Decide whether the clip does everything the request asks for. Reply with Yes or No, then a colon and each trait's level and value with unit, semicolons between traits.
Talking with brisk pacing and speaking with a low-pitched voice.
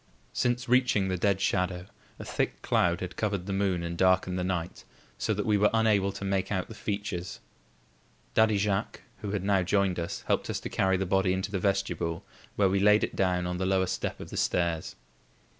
Yes: fast, 210 wpm; very low, 95 Hz